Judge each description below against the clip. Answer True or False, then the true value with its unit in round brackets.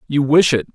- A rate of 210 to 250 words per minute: True (240 wpm)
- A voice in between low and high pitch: True (145 Hz)